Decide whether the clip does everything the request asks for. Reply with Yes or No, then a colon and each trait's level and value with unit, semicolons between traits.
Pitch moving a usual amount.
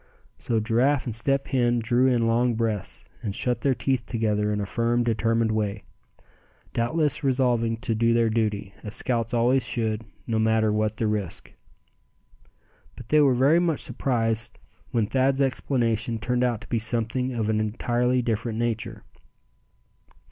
No: narrow, 2.2 semitones